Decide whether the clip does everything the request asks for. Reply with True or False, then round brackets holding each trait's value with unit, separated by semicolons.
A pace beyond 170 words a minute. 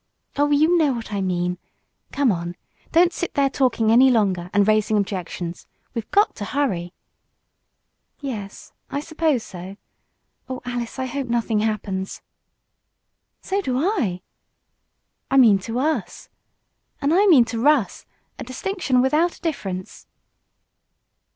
False (135 wpm)